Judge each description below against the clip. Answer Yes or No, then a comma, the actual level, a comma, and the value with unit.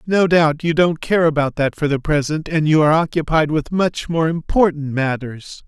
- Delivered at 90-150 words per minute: No, average, 200 wpm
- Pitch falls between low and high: Yes, medium, 155 Hz